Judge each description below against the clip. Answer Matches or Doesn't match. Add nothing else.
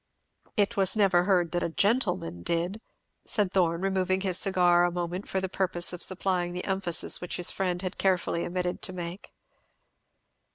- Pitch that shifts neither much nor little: Doesn't match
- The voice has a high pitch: Doesn't match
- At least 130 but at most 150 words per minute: Doesn't match